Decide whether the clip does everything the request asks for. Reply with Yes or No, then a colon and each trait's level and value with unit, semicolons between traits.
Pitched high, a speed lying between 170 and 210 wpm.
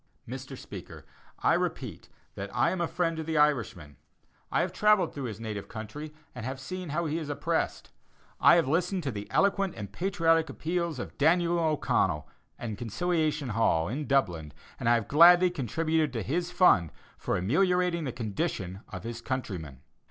No: medium, 145 Hz; average, 175 wpm